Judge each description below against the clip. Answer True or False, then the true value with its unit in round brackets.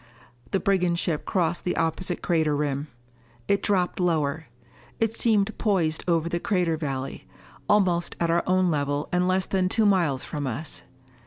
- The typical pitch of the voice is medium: True (170 Hz)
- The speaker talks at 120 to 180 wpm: True (160 wpm)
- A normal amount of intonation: True (3.2 semitones)